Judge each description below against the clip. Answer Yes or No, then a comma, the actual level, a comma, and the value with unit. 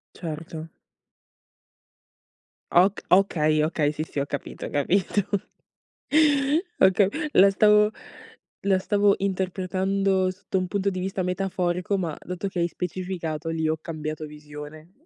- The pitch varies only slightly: No, average, 3.5 semitones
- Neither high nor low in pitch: Yes, medium, 180 Hz